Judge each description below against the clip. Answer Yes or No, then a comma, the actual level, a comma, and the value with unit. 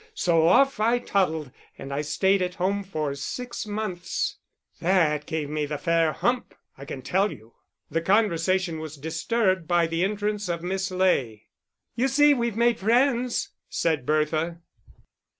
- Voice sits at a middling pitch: Yes, medium, 180 Hz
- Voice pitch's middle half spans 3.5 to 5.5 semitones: Yes, average, 5.0 semitones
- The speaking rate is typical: Yes, average, 150 wpm